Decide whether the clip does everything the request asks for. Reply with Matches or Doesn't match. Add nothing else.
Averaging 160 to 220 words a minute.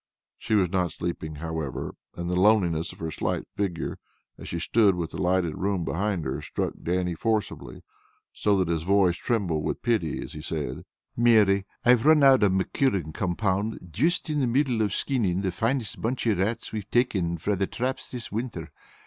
Matches